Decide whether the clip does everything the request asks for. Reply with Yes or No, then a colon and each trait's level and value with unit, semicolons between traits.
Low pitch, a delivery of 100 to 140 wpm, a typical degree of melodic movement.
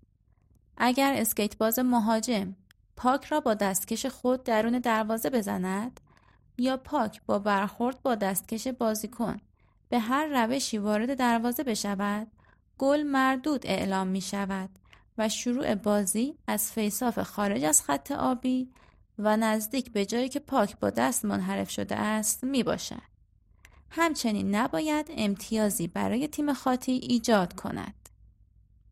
No: high, 225 Hz; average, 125 wpm; average, 4.1 semitones